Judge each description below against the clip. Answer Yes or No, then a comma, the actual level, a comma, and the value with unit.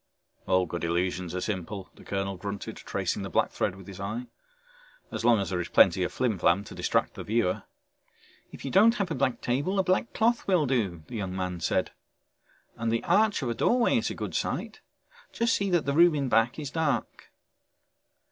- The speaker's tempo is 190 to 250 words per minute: Yes, fast, 205 wpm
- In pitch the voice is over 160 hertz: No, low, 115 Hz